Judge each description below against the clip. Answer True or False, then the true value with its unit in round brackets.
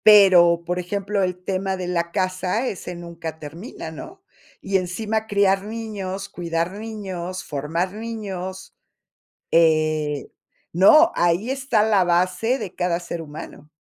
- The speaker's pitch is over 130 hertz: True (185 Hz)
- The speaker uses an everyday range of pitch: True (3.2 semitones)